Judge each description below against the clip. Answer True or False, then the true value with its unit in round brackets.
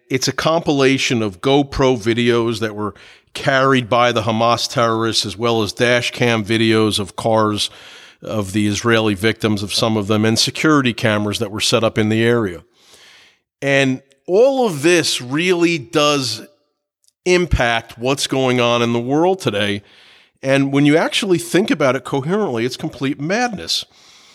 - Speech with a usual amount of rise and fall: True (4.2 semitones)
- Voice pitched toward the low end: True (120 Hz)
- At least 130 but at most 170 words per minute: True (160 wpm)